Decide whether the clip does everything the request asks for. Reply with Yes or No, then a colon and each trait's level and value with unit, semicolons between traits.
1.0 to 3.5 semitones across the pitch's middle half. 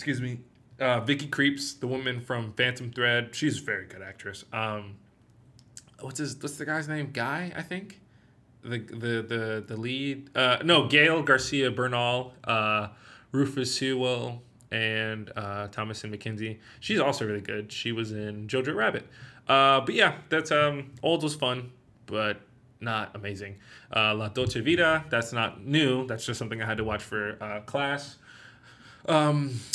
No: average, 3.9 semitones